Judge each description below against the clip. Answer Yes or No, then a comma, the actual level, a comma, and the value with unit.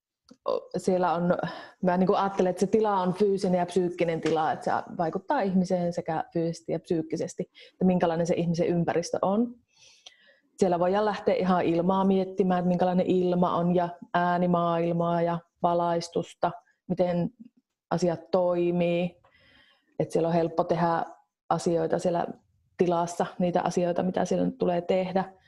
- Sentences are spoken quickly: No, average, 140 wpm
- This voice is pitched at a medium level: Yes, medium, 180 Hz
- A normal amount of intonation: No, narrow, 1.8 semitones